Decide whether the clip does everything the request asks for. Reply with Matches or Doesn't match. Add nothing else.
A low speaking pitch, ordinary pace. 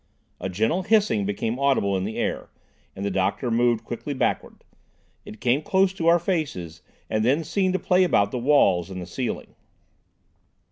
Matches